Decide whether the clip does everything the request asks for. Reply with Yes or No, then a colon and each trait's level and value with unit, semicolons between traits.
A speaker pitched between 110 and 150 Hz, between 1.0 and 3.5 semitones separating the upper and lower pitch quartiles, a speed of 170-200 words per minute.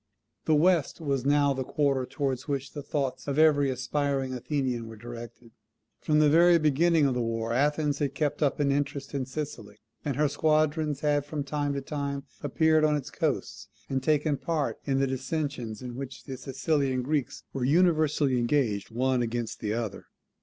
Yes: medium, 140 Hz; narrow, 2.6 semitones; average, 180 wpm